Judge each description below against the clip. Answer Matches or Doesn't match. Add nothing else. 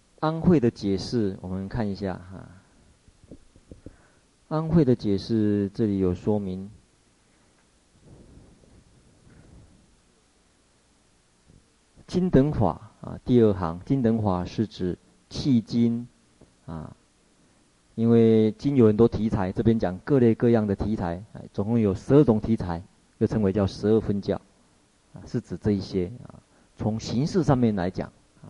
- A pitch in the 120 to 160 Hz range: Doesn't match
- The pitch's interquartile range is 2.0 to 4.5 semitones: Matches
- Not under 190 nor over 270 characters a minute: Doesn't match